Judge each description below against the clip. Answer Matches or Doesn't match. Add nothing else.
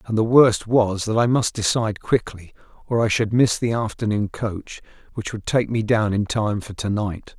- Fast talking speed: Matches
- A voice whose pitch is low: Matches